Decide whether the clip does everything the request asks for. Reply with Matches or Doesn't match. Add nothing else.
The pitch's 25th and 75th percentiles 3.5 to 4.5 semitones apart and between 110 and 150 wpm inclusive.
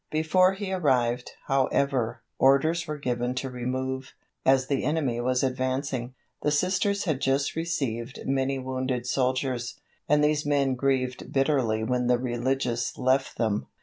Doesn't match